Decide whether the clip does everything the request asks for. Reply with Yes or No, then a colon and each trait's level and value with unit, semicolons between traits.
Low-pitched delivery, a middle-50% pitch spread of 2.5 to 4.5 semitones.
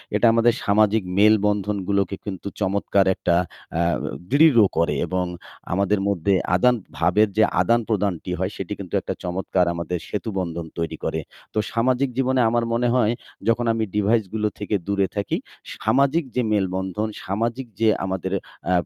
Yes: low, 105 Hz; average, 3.4 semitones